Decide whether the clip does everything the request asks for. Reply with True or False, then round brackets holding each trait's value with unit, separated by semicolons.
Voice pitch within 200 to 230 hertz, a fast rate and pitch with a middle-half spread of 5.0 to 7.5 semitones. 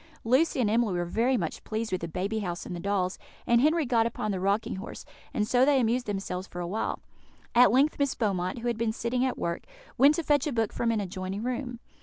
False (225 Hz; 240 wpm; 4.4 semitones)